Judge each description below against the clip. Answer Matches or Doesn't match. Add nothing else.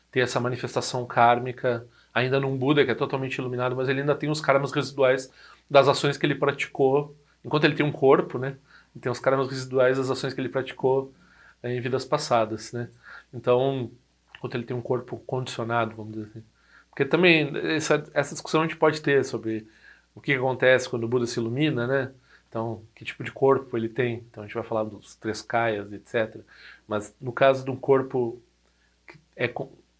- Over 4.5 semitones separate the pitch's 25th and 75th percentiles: Doesn't match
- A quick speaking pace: Matches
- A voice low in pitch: Matches